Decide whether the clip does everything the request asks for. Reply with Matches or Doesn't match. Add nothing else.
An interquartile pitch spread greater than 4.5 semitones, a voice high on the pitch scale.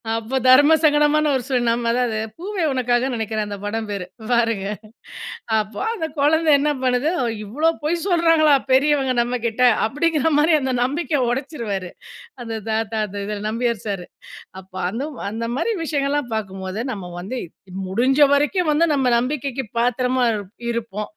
Matches